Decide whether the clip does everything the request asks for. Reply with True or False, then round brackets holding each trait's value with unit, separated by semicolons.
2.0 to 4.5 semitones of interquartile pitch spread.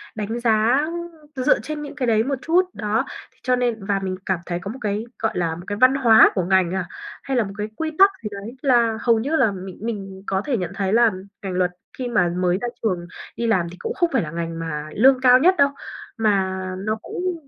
False (5.1 semitones)